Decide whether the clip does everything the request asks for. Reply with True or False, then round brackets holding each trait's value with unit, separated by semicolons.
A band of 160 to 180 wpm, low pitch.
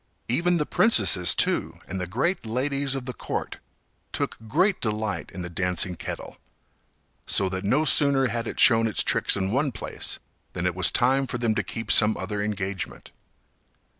True (175 wpm; 115 Hz)